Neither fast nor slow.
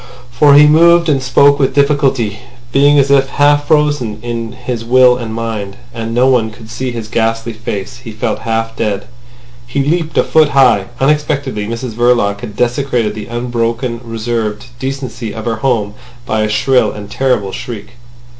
Yes: average, 165 wpm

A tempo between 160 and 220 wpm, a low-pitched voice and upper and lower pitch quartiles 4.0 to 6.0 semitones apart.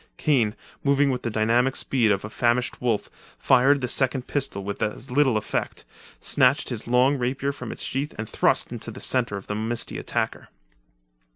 No: average, 180 wpm; low, 125 Hz; average, 3.4 semitones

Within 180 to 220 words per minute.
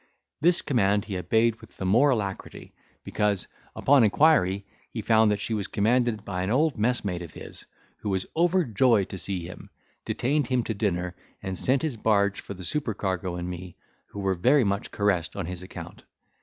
Yes: average, 185 wpm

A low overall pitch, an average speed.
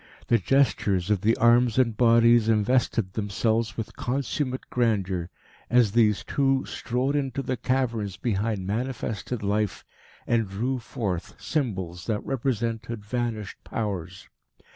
No: low, 115 Hz; slow, 120 wpm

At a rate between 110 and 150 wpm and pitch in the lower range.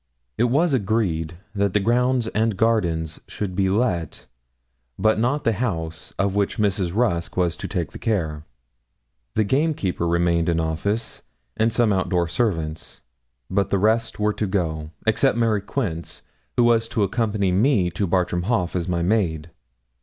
No: average, 160 wpm; low, 100 Hz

